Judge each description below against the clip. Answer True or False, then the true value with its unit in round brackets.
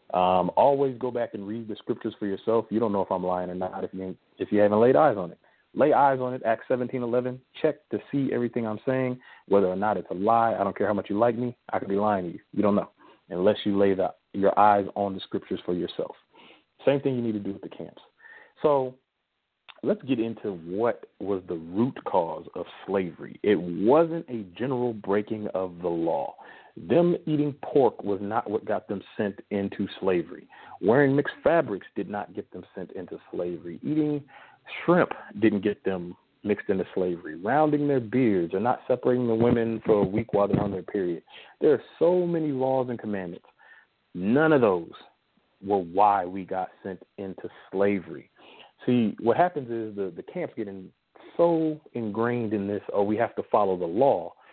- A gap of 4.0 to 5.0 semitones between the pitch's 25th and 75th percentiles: True (4.7 semitones)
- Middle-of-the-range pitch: False (115 Hz)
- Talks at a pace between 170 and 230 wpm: True (200 wpm)